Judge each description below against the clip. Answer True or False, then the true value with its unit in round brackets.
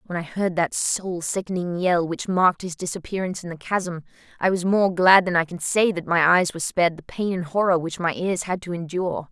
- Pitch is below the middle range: False (175 Hz)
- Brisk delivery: True (240 wpm)